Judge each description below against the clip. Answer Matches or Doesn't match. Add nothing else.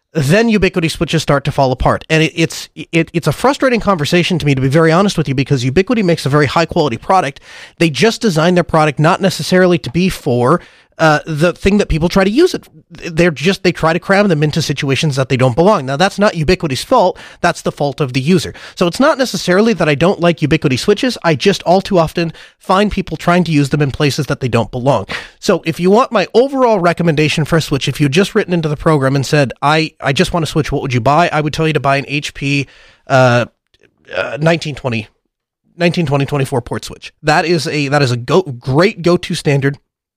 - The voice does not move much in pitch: Doesn't match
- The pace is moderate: Doesn't match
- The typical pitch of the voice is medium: Matches